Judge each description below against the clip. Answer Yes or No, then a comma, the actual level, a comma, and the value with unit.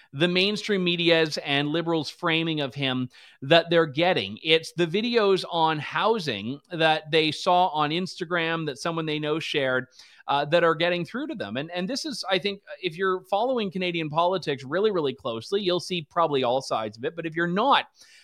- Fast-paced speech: No, average, 190 wpm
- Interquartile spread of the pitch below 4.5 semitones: Yes, average, 2.9 semitones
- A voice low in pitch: No, medium, 170 Hz